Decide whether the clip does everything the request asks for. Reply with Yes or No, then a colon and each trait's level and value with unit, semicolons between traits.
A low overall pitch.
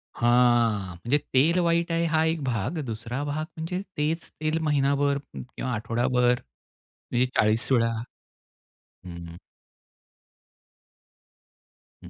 Yes: low, 130 Hz